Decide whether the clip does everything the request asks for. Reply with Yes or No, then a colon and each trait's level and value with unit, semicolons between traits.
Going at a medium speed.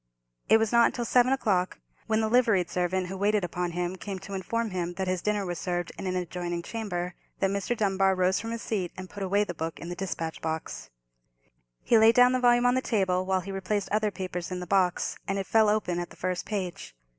No: fast, 235 wpm